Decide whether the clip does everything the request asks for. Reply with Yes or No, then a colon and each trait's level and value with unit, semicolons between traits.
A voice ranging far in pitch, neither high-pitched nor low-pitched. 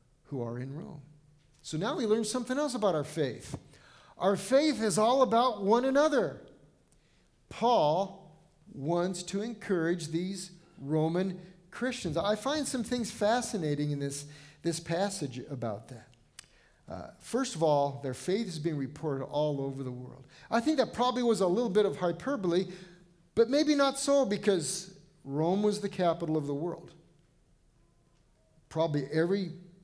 Yes: wide, 6.5 semitones; medium, 180 Hz